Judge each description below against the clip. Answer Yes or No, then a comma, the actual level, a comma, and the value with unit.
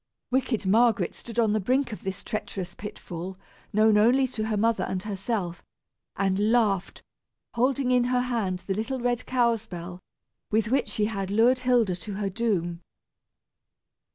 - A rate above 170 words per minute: No, average, 160 wpm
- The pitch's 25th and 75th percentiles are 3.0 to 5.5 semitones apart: Yes, average, 3.9 semitones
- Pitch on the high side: Yes, high, 215 Hz